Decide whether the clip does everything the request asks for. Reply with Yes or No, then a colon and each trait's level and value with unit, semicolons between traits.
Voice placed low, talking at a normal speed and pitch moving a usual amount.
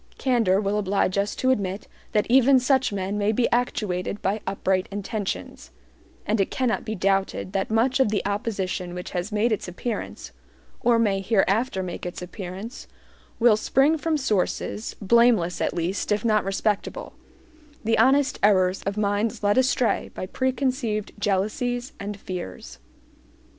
No: high, 210 Hz; average, 150 wpm; average, 3.7 semitones